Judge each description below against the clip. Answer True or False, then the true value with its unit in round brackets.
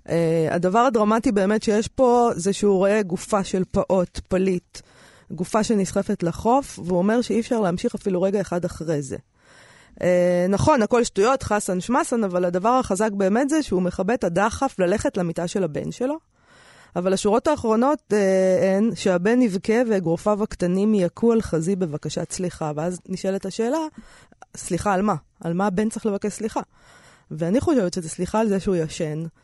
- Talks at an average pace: False (165 wpm)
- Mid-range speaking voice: False (195 Hz)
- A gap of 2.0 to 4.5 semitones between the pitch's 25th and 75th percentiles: True (3.7 semitones)